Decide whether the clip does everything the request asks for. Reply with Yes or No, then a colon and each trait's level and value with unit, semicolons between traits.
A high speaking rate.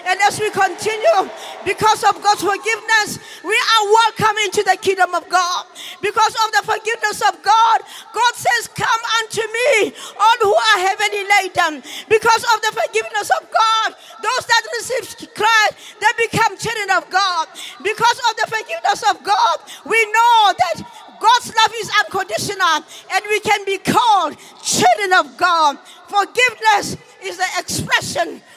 No: average, 150 wpm